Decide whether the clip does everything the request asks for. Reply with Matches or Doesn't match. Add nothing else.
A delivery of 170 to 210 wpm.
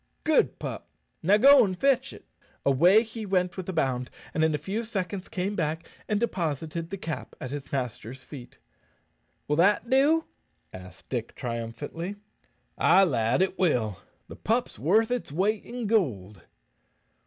Doesn't match